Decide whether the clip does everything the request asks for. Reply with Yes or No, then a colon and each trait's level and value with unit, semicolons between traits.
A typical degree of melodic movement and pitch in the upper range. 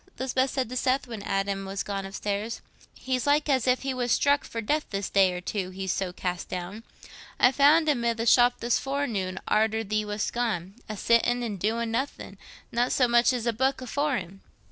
Yes: average, 4.6 semitones; high, 230 Hz